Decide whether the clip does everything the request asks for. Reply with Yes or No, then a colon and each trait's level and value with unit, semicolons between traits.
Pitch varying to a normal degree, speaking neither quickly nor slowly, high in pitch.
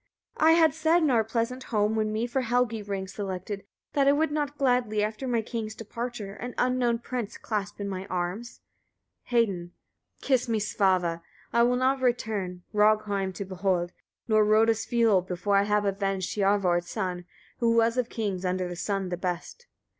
Yes: average, 3.7 semitones; average, 175 wpm; high, 215 Hz